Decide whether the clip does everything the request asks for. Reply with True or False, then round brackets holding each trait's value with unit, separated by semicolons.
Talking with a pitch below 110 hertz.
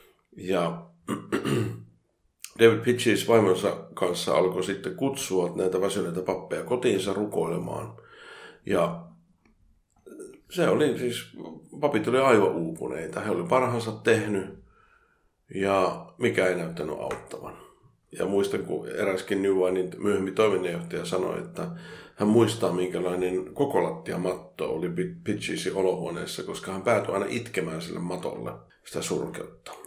True (100 Hz)